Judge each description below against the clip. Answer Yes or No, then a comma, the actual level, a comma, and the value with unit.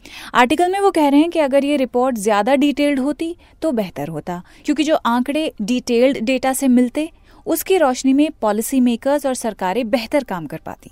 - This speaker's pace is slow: No, average, 185 wpm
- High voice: Yes, very high, 265 Hz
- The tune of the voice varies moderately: Yes, average, 4.0 semitones